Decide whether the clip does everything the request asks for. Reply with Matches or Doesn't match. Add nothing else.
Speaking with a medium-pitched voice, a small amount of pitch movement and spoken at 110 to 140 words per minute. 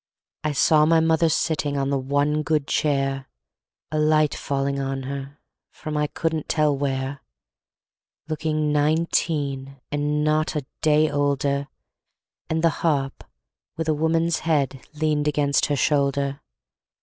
Matches